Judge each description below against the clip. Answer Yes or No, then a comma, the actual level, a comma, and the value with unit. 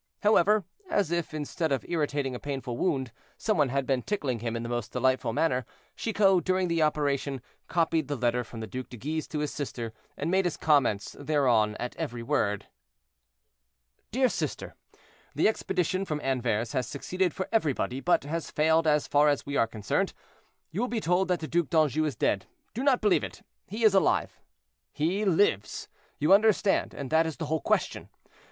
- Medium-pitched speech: Yes, medium, 150 Hz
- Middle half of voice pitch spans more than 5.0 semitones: Yes, wide, 5.6 semitones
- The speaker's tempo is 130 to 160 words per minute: No, average, 185 wpm